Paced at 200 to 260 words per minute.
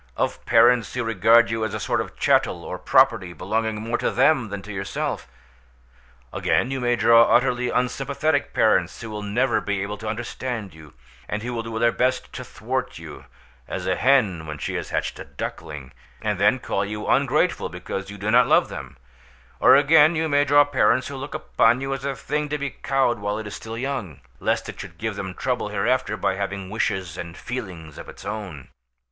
Yes: fast, 205 wpm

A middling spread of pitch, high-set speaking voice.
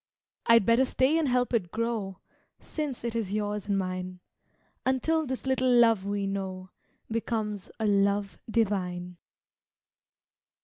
Yes: average, 3.8 semitones; high, 215 Hz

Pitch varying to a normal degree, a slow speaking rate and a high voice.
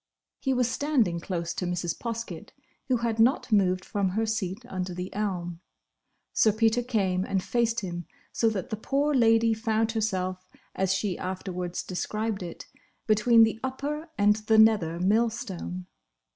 No: average, 3.7 semitones; average, 155 wpm; high, 215 Hz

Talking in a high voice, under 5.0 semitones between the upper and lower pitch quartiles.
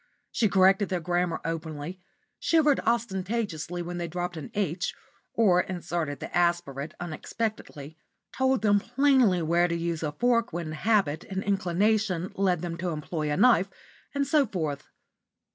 No: medium, 180 Hz; average, 4.2 semitones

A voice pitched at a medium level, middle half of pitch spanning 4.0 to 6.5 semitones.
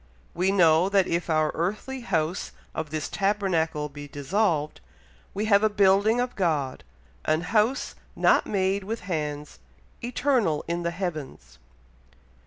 Yes: medium, 180 Hz; average, 4.7 semitones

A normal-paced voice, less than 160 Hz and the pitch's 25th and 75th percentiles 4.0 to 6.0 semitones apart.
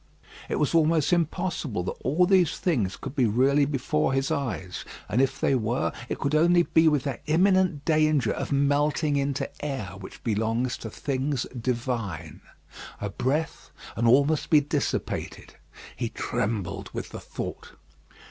Yes: average, 155 wpm; medium, 140 Hz; average, 4.5 semitones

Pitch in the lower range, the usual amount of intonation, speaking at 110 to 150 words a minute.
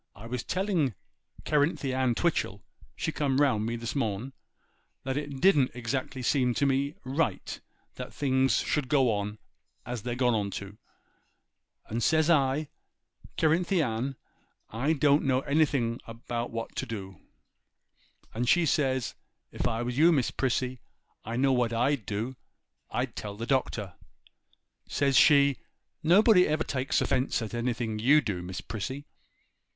Yes: low, 130 Hz; average, 3.7 semitones; average, 145 wpm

